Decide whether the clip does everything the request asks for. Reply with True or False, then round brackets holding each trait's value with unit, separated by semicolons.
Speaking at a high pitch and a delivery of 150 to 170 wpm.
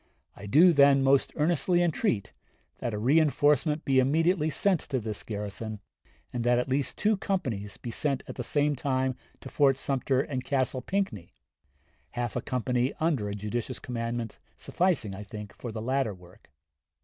False (130 Hz; 165 wpm)